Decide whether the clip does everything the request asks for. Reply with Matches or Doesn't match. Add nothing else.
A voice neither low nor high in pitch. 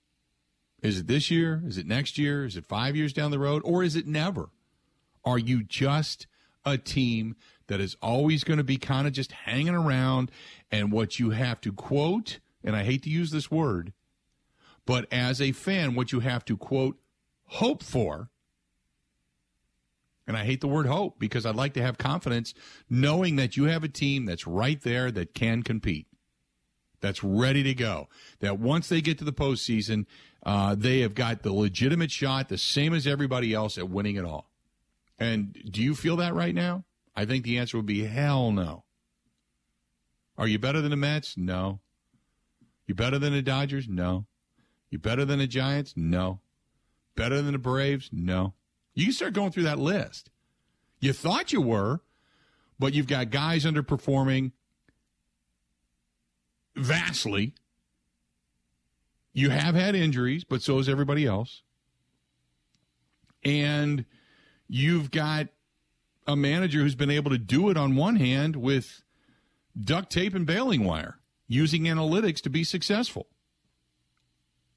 Doesn't match